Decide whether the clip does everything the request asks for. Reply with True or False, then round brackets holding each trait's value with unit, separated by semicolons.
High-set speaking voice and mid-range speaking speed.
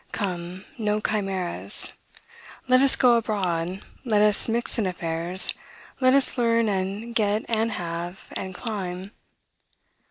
False (205 Hz; 125 wpm)